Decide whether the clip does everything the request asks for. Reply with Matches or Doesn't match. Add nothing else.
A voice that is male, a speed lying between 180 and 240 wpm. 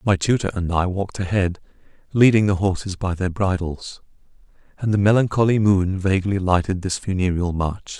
Doesn't match